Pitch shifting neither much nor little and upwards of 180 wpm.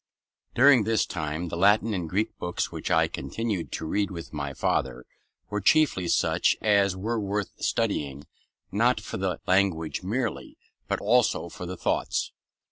No: average, 4.0 semitones; average, 155 wpm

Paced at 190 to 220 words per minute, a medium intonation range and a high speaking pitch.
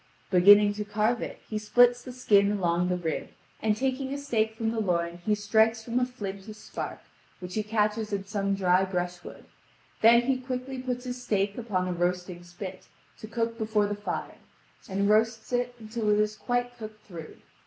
Yes: average, 195 wpm; average, 3.3 semitones; high, 215 Hz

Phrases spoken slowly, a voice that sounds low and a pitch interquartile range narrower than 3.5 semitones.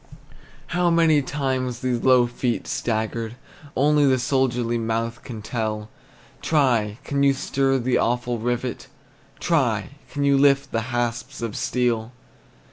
Yes: slow, 130 wpm; low, 125 Hz; average, 2.9 semitones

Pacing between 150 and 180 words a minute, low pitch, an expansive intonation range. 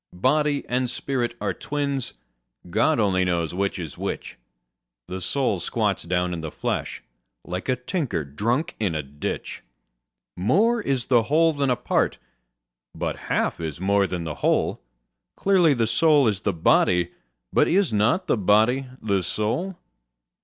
Yes: average, 155 wpm; low, 110 Hz; wide, 7.6 semitones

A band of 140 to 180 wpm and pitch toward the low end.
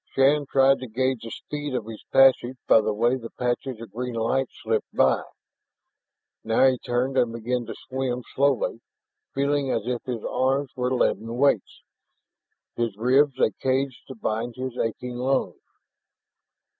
Yes: average, 155 wpm; low, 125 Hz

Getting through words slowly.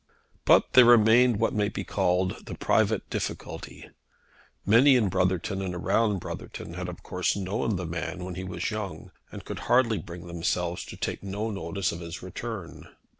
No: average, 175 wpm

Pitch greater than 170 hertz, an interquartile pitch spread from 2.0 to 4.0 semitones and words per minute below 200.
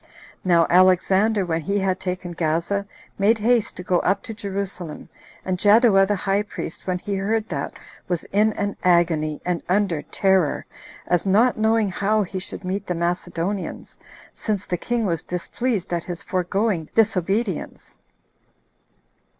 Yes: high, 190 Hz; average, 2.7 semitones; average, 150 wpm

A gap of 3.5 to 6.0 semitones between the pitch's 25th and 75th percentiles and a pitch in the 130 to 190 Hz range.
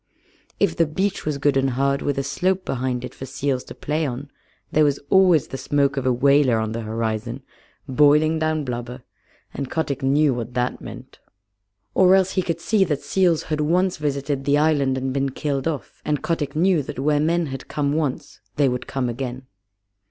No: average, 3.0 semitones; medium, 140 Hz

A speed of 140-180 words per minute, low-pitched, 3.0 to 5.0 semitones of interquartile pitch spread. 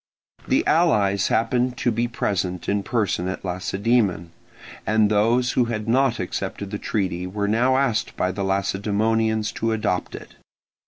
Yes: average, 150 wpm; low, 105 Hz; average, 3.3 semitones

